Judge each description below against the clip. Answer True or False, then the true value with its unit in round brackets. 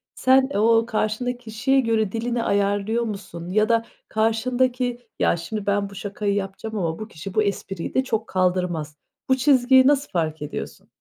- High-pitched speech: True (220 Hz)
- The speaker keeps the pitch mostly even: False (3.7 semitones)